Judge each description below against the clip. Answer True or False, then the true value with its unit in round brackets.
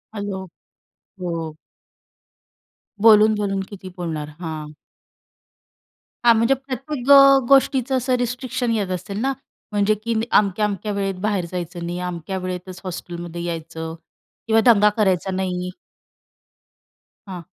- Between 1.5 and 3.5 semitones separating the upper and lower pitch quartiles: False (4.3 semitones)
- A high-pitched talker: True (195 Hz)